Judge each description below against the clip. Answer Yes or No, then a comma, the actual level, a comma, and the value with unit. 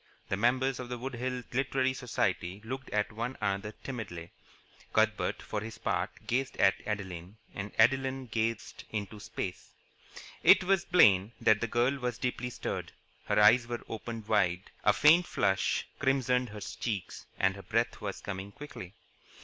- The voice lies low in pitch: Yes, low, 115 Hz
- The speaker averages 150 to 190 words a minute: Yes, average, 155 wpm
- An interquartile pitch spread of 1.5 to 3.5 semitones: No, average, 4.0 semitones